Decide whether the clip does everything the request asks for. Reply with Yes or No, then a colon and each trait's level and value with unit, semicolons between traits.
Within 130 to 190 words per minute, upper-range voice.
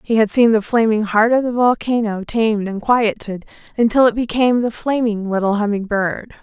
Yes: average, 185 wpm; high, 220 Hz